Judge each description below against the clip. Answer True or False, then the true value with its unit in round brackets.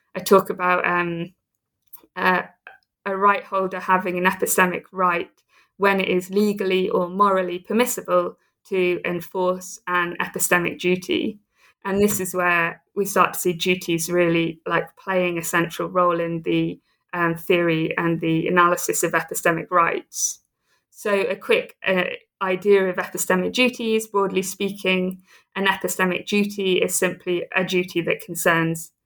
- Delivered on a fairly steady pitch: True (1.9 semitones)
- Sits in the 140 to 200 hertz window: True (185 Hz)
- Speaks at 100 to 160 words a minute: True (140 wpm)